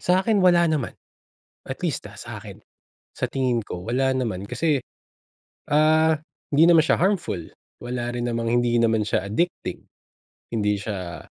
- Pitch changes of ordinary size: No, wide, 6.1 semitones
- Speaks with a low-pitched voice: Yes, low, 125 Hz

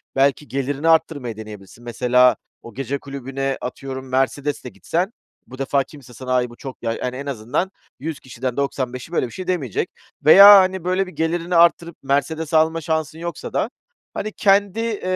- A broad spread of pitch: No, average, 4.6 semitones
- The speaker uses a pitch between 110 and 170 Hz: Yes, medium, 140 Hz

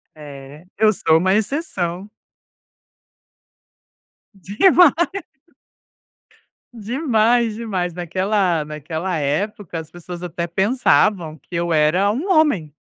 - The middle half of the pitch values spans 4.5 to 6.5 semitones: Yes, average, 5.0 semitones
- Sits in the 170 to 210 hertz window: Yes, medium, 185 Hz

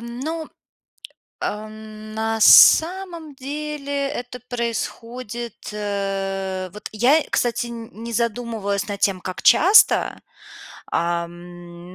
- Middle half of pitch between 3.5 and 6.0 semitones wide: Yes, average, 4.2 semitones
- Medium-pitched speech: No, high, 225 Hz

